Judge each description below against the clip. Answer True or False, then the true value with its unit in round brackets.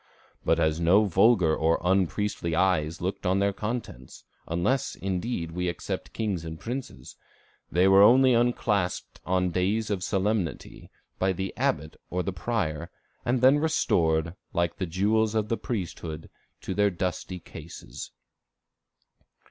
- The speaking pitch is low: True (95 Hz)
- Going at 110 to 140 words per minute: True (135 wpm)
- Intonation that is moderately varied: True (4.1 semitones)